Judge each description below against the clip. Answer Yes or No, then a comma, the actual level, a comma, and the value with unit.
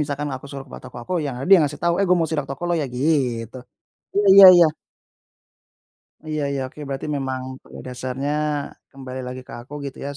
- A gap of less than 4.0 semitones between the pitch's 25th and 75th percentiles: Yes, average, 2.7 semitones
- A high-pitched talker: No, medium, 140 Hz